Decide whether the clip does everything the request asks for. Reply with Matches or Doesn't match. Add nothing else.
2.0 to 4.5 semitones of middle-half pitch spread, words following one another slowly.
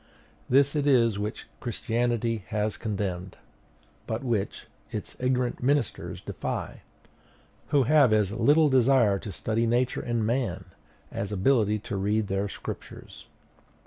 Matches